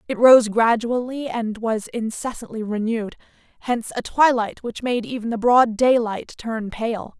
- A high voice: Yes, high, 230 Hz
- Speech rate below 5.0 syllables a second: Yes, 4.6 syllables/s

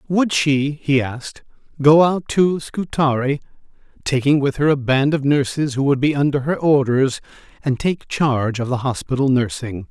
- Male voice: Yes, male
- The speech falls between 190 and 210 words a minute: No, average, 170 wpm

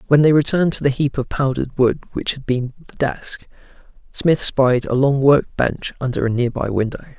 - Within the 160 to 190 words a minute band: No, average, 200 wpm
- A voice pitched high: No, low, 135 Hz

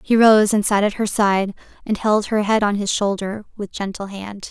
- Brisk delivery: Yes, fast, 225 wpm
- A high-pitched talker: Yes, high, 205 Hz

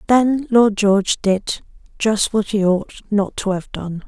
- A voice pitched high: Yes, high, 210 Hz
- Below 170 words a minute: Yes, average, 160 wpm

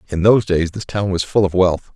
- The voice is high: No, very low, 95 Hz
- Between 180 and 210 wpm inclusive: No, fast, 275 wpm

